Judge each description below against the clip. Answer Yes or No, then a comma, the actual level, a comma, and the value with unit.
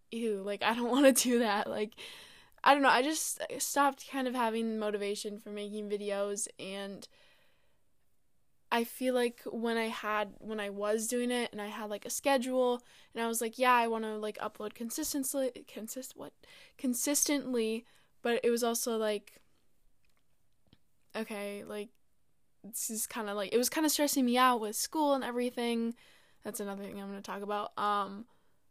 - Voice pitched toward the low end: No, high, 230 Hz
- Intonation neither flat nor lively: Yes, average, 3.2 semitones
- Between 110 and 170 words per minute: No, average, 180 wpm